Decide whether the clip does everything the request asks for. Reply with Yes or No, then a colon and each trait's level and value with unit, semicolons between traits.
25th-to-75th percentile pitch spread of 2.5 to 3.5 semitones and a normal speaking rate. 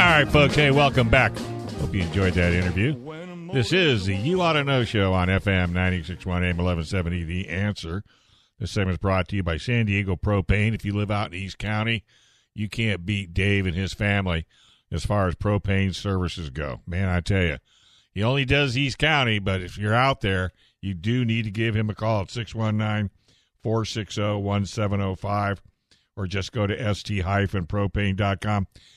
Yes: average, 3.0 semitones; average, 175 wpm